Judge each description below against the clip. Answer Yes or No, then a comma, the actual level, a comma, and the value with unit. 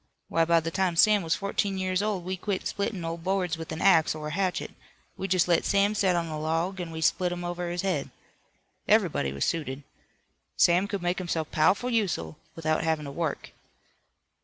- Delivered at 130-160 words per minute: No, average, 200 wpm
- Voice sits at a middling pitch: Yes, medium, 175 Hz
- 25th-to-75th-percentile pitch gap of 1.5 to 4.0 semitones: Yes, average, 2.9 semitones